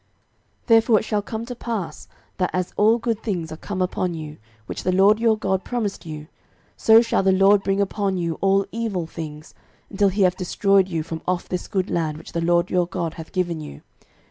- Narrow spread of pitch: No, average, 3.4 semitones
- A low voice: No, high, 190 Hz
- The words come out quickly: Yes, fast, 215 wpm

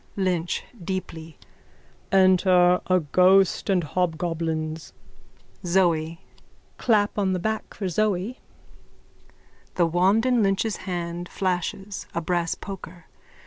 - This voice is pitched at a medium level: Yes, medium, 180 Hz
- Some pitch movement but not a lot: No, narrow, 2.3 semitones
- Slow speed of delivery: Yes, slow, 100 wpm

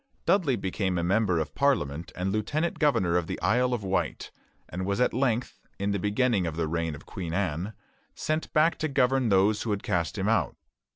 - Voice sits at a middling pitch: No, low, 100 Hz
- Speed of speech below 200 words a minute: No, fast, 205 wpm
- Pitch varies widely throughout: Yes, wide, 6.1 semitones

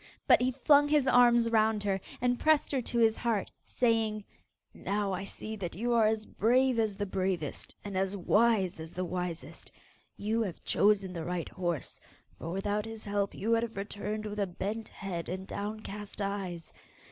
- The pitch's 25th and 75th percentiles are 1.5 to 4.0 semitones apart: Yes, average, 3.1 semitones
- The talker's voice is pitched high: Yes, high, 210 Hz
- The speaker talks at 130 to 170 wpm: No, average, 180 wpm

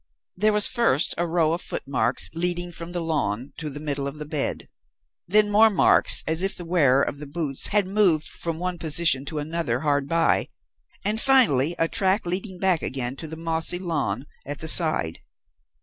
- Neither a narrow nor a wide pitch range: Yes, average, 3.8 semitones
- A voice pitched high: No, medium, 165 Hz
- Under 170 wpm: No, average, 190 wpm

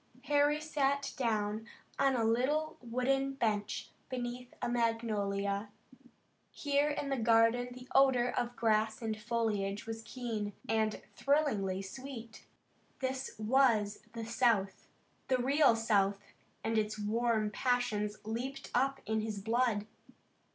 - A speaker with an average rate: No, slow, 125 wpm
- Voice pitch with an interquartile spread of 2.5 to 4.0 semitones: Yes, average, 3.3 semitones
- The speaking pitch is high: Yes, high, 230 Hz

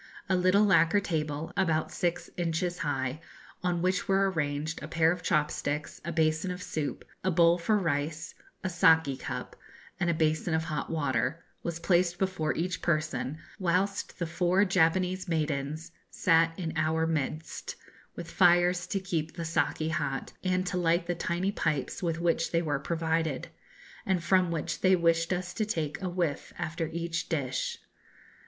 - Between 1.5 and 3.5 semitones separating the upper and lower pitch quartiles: Yes, narrow, 2.4 semitones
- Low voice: No, medium, 165 Hz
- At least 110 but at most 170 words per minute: Yes, average, 165 wpm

